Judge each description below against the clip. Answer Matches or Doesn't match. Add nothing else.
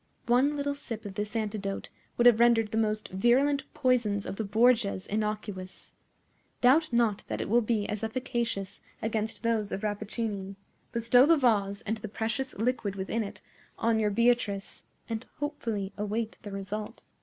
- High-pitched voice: Matches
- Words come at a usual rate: Matches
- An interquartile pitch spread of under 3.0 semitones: Matches